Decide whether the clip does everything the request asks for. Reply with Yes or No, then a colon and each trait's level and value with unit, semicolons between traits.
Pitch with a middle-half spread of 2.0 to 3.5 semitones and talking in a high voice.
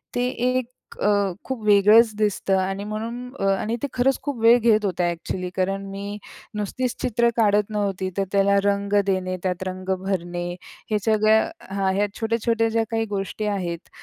Yes: average, 2.8 semitones; high, 205 Hz